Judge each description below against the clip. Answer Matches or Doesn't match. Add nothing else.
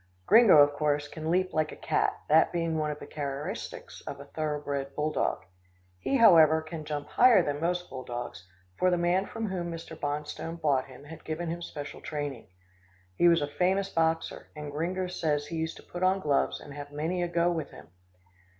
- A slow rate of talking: Doesn't match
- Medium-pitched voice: Matches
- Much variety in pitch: Doesn't match